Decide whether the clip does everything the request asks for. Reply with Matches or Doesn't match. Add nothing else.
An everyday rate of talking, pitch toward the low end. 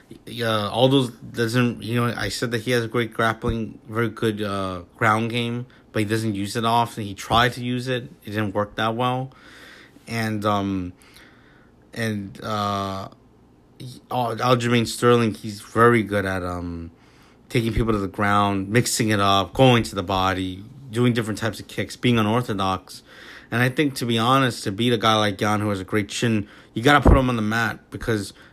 Matches